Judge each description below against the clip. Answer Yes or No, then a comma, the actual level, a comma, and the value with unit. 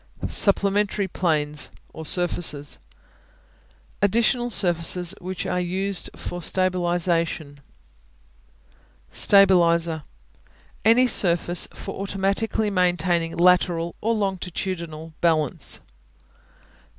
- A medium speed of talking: No, slow, 75 wpm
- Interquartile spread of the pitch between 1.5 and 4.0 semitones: Yes, average, 2.7 semitones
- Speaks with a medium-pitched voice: Yes, medium, 180 Hz